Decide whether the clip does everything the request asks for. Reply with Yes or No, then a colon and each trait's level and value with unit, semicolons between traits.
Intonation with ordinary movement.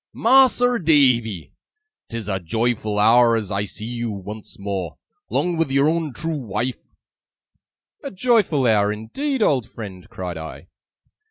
No: wide, 7.4 semitones